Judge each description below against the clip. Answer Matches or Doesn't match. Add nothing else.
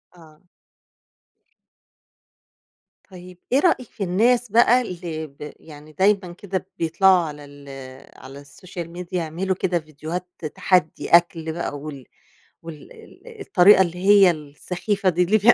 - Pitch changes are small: Doesn't match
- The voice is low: Doesn't match